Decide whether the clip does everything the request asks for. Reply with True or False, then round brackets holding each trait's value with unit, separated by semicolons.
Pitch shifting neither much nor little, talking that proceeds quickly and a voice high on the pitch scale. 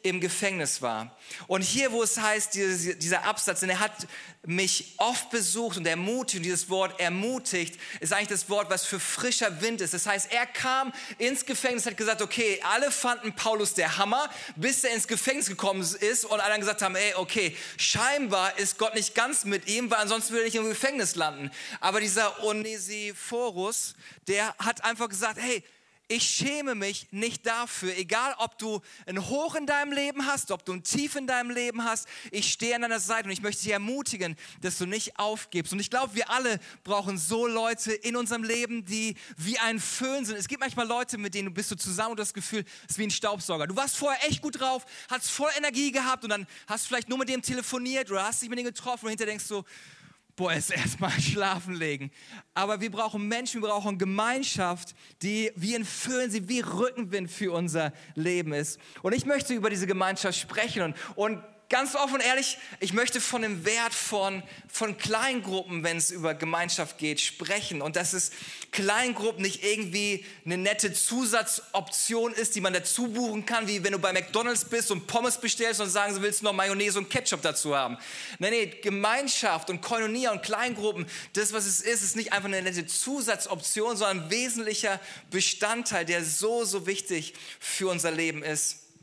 True (3.7 semitones; 200 wpm; 210 Hz)